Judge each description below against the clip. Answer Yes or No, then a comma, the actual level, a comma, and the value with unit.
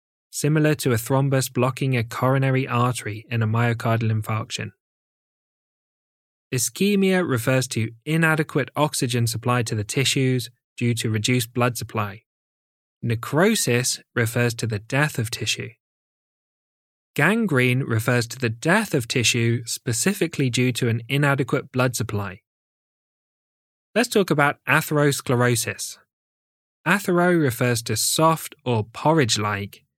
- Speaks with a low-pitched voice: Yes, low, 125 Hz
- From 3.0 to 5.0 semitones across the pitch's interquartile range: Yes, average, 3.8 semitones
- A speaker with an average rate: No, slow, 115 wpm